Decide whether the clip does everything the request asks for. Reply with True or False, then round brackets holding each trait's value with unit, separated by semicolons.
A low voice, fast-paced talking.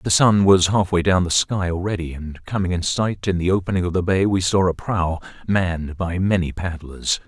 True (90 Hz; 215 wpm)